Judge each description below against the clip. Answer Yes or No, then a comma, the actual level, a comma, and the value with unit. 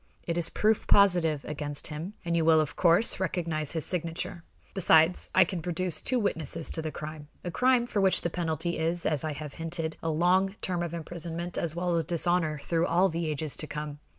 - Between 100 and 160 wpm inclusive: No, fast, 205 wpm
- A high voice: No, medium, 165 Hz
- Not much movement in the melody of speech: Yes, narrow, 2.2 semitones